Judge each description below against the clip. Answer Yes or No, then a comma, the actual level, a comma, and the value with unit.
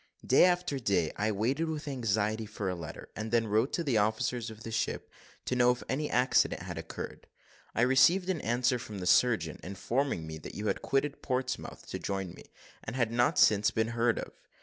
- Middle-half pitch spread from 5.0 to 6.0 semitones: No, average, 3.9 semitones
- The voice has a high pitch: No, low, 115 Hz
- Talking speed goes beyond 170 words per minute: Yes, fast, 205 wpm